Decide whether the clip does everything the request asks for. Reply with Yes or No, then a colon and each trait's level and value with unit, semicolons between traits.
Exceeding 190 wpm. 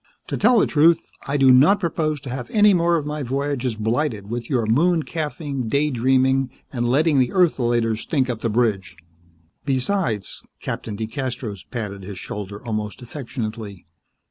No: average, 165 wpm